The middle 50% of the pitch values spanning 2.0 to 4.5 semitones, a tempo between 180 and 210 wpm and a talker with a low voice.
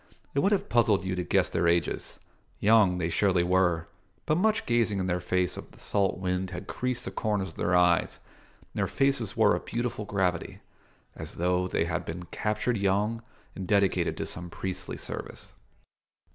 Yes: average, 3.5 semitones; average, 185 wpm; very low, 95 Hz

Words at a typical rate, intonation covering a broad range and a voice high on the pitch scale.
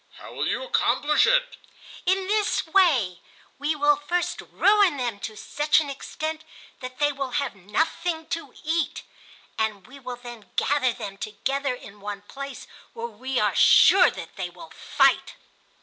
Yes: average, 160 wpm; wide, 5.7 semitones; very high, 275 Hz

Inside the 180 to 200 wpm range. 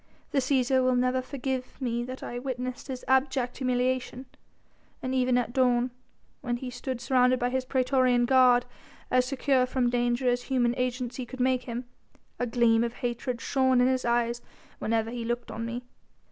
No: average, 170 wpm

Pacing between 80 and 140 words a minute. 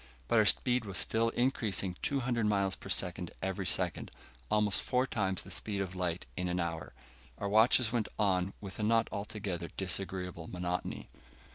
No: average, 165 wpm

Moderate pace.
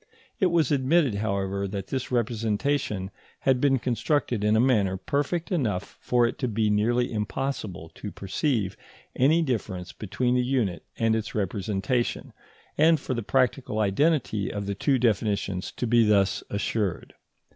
Yes: average, 150 wpm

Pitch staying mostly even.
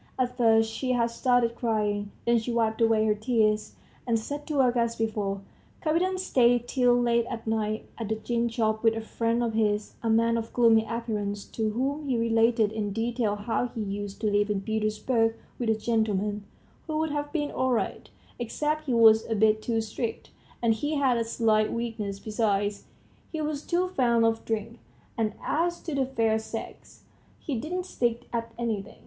Yes: narrow, 2.1 semitones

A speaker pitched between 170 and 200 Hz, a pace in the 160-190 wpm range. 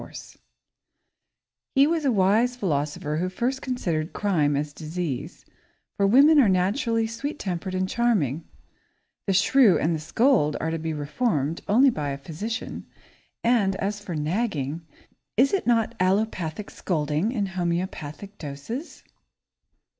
No: high, 190 Hz; average, 140 wpm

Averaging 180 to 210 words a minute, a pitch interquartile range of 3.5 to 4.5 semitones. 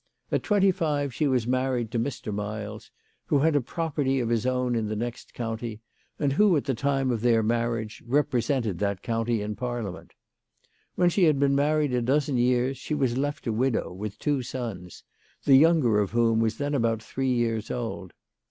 Yes: average, 190 wpm; average, 3.8 semitones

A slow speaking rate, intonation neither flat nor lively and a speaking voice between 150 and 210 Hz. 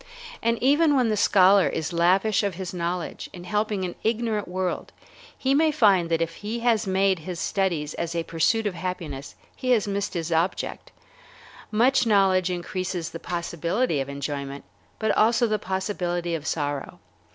No: average, 165 wpm; average, 4.1 semitones; medium, 185 Hz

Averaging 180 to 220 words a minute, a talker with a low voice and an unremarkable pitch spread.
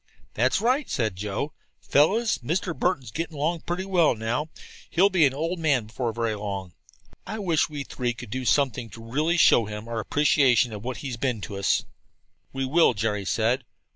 No: average, 185 wpm; low, 130 Hz; wide, 6.4 semitones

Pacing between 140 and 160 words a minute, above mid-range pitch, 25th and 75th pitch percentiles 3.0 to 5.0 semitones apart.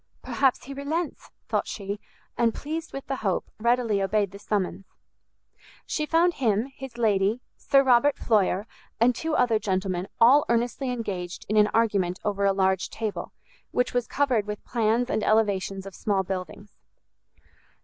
Yes: average, 155 wpm; high, 220 Hz; average, 4.1 semitones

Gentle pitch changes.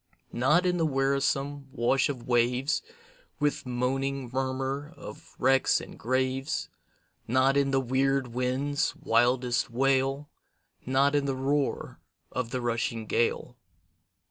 Yes: narrow, 1.6 semitones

